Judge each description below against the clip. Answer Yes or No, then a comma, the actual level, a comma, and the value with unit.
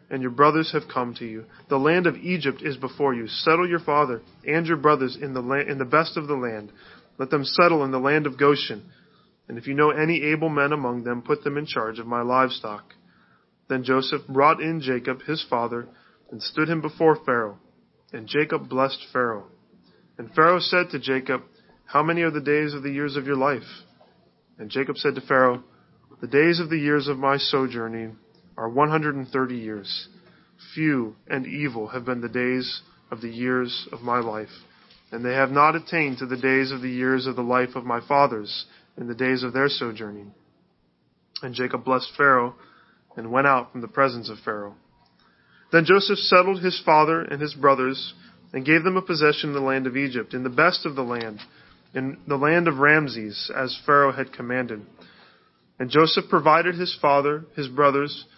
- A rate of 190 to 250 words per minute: Yes, average, 195 wpm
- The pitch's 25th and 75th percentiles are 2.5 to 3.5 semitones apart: Yes, average, 3.2 semitones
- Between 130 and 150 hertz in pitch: Yes, low, 135 Hz